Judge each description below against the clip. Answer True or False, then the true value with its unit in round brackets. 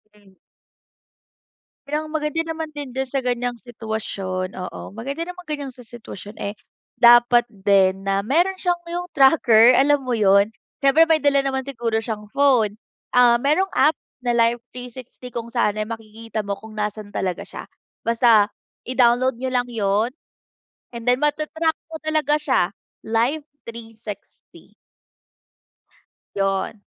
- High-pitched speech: True (240 Hz)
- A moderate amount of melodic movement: True (4.5 semitones)